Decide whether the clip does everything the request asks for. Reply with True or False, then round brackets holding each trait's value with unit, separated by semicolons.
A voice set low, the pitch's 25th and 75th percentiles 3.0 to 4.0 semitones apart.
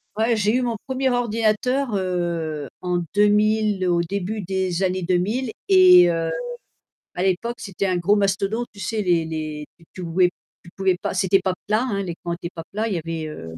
False (190 Hz; 3.6 semitones)